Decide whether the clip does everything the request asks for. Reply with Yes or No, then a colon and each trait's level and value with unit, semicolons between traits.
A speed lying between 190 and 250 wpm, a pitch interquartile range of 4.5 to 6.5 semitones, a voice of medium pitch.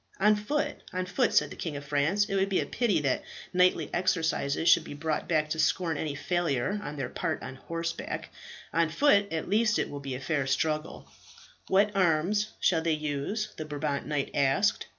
Yes: average, 195 wpm; average, 5.0 semitones; medium, 165 Hz